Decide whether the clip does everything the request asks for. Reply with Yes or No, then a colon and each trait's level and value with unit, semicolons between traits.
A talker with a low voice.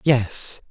Yes: low, 125 Hz